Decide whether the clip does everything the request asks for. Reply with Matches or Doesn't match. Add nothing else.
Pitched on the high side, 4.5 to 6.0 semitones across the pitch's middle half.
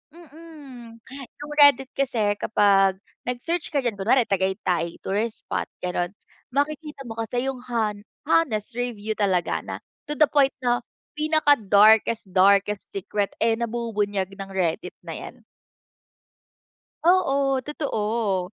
Matches